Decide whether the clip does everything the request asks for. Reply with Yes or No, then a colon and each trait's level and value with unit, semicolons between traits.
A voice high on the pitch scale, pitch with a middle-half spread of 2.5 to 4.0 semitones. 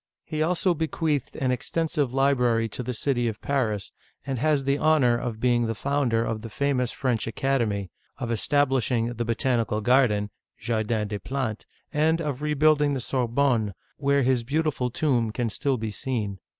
No: low, 125 Hz; average, 3.7 semitones